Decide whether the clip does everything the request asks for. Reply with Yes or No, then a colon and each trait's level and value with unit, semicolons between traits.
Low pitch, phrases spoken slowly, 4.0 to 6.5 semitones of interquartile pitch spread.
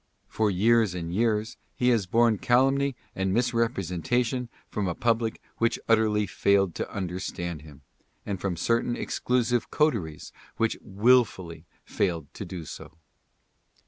Yes: low, 105 Hz; slow, 130 wpm; average, 4.7 semitones